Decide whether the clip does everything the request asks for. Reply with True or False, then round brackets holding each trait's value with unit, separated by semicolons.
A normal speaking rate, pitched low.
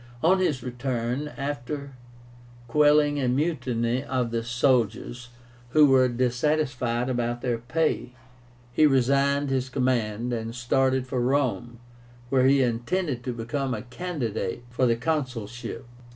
False (125 wpm; 130 Hz)